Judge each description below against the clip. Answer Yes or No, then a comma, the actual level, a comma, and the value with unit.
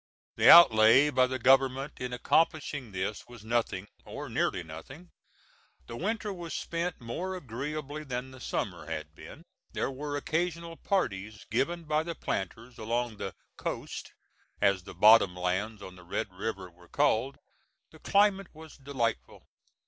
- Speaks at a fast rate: No, average, 150 wpm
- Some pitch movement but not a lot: No, wide, 6.4 semitones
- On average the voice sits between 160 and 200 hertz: No, low, 125 Hz